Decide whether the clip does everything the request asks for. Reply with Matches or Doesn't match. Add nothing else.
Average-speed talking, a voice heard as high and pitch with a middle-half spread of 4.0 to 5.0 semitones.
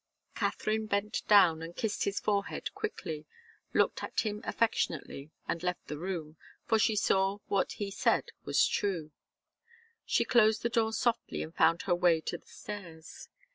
Matches